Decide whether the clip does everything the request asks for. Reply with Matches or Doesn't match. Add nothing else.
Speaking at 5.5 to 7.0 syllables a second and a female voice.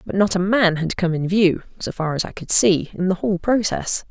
Doesn't match